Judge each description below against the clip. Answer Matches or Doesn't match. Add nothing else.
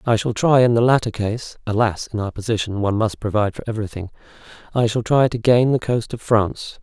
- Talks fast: Matches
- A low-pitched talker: Matches